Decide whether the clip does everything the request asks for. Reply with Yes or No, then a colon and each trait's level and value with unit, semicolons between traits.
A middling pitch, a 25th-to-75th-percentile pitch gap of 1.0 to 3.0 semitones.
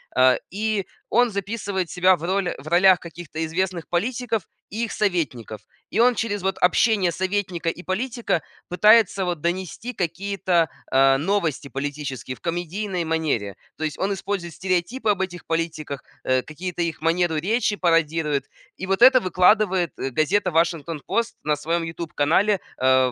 No: medium, 175 Hz; average, 3.8 semitones